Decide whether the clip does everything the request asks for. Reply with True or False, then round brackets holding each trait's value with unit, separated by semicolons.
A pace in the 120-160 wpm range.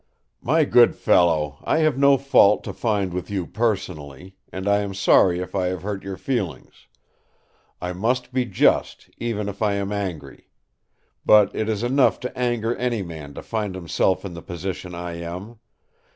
False (175 wpm)